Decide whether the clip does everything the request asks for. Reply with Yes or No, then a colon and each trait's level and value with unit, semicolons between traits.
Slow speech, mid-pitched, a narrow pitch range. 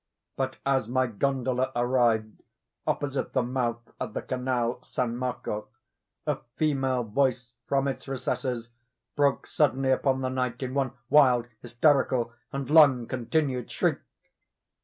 No: slow, 130 wpm; low, 130 Hz; narrow, 2.0 semitones